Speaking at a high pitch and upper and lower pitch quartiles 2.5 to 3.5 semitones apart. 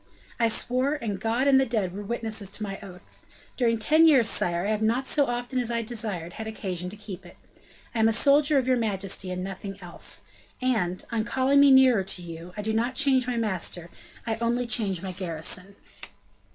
No: high, 220 Hz; average, 4.5 semitones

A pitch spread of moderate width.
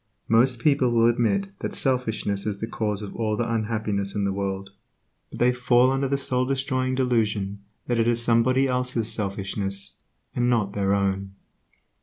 Yes: average, 4.0 semitones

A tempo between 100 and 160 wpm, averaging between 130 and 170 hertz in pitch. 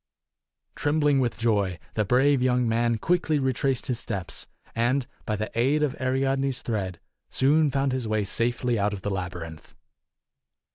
No: average, 150 wpm; low, 120 Hz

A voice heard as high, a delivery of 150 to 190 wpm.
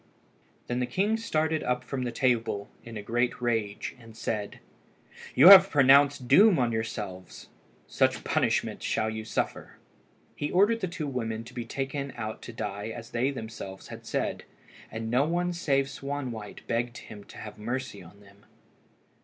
No: low, 120 Hz; average, 165 wpm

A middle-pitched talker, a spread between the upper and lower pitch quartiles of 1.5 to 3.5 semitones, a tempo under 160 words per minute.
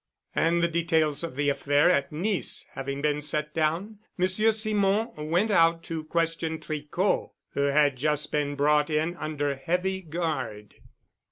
Yes: medium, 155 Hz; average, 2.9 semitones; average, 150 wpm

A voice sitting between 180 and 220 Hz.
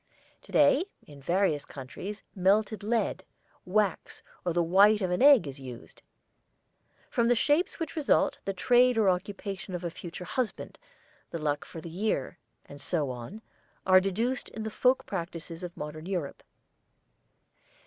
Yes: medium, 185 Hz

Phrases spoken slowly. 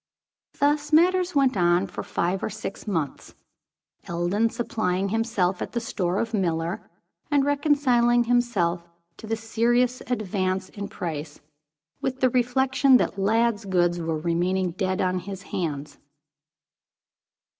Yes: slow, 130 wpm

